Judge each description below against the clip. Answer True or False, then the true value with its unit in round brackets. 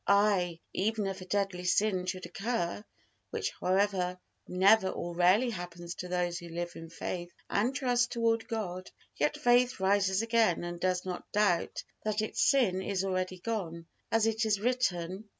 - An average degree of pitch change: True (3.6 semitones)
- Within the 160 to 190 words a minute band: True (170 wpm)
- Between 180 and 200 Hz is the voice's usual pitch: True (190 Hz)